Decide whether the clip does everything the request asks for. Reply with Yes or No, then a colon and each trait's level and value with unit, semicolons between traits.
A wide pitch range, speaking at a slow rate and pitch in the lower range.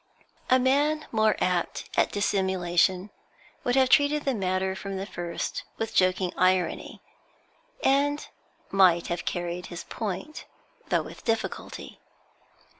No: wide, 6.0 semitones; slow, 120 wpm; high, 195 Hz